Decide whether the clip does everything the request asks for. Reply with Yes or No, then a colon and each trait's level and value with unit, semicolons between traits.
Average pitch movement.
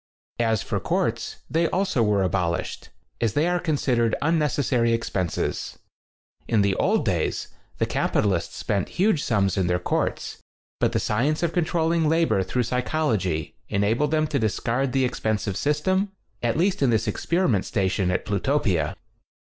No: wide, 7.6 semitones